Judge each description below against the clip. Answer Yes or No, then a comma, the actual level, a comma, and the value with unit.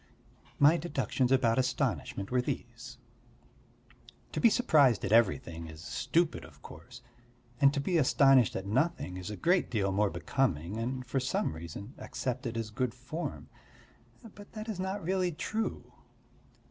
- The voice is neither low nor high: No, low, 125 Hz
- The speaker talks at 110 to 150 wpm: Yes, average, 145 wpm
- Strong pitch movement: Yes, wide, 6.6 semitones